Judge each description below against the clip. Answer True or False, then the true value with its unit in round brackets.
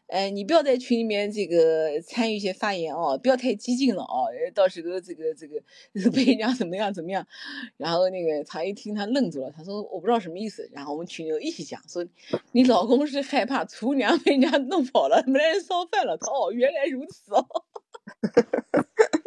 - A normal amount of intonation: False (7.3 semitones)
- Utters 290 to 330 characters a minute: True (300 characters per minute)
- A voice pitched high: True (235 Hz)